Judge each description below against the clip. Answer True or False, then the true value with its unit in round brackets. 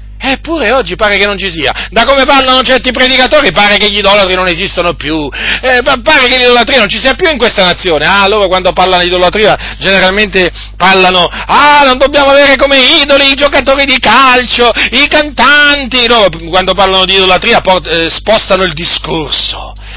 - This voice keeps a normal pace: False (185 wpm)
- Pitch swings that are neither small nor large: False (6.4 semitones)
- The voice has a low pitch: False (215 Hz)